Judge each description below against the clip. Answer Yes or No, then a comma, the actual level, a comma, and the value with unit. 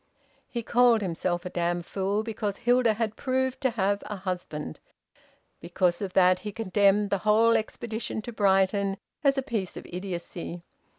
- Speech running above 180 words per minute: No, average, 160 wpm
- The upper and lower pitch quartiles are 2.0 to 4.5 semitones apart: Yes, average, 3.7 semitones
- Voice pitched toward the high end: Yes, high, 205 Hz